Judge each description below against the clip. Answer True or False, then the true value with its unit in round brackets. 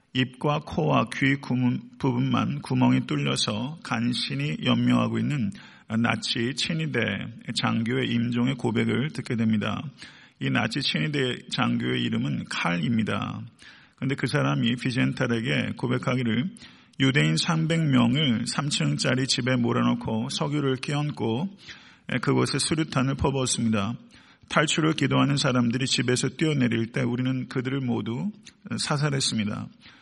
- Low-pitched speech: True (130 Hz)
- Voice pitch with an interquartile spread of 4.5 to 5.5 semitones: False (3.3 semitones)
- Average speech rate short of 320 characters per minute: True (280 characters per minute)